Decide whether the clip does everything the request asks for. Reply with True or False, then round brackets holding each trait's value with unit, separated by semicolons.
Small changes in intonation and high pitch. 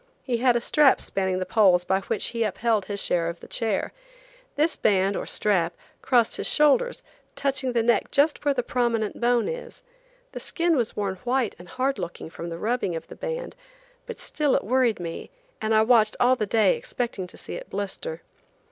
False (5.2 semitones; 230 Hz)